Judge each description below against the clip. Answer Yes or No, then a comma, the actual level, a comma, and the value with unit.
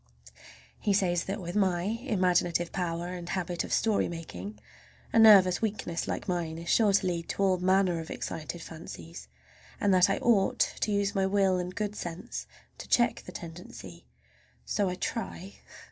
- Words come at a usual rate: Yes, average, 170 wpm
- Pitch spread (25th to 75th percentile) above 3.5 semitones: No, average, 2.8 semitones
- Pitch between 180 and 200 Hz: Yes, medium, 185 Hz